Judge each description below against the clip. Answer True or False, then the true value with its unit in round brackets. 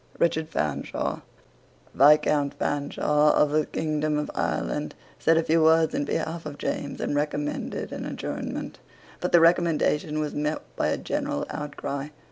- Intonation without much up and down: True (1.5 semitones)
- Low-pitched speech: False (150 Hz)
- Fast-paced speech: False (145 wpm)